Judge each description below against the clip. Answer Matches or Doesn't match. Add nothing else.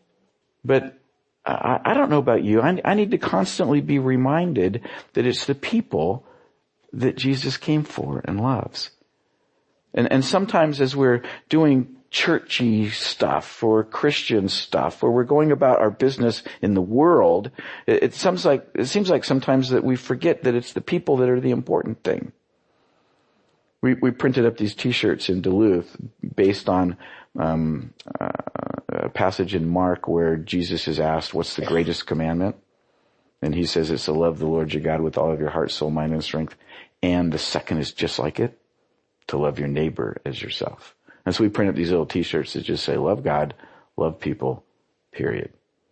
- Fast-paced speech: Doesn't match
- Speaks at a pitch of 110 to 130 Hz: Matches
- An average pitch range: Doesn't match